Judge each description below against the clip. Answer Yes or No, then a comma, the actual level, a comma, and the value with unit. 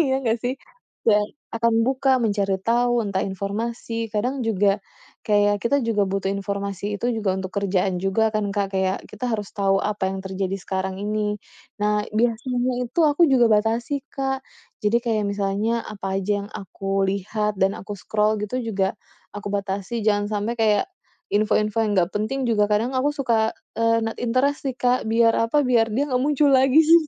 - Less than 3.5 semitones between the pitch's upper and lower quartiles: Yes, average, 3.0 semitones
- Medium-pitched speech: No, high, 215 Hz